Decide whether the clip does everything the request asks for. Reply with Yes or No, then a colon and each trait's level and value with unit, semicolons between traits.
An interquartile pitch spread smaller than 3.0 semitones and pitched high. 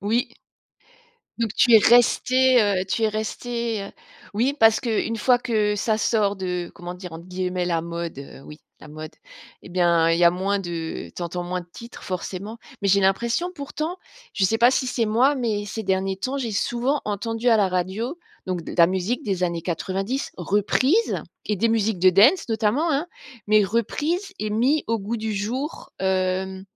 No: average, 4.3 semitones; high, 210 Hz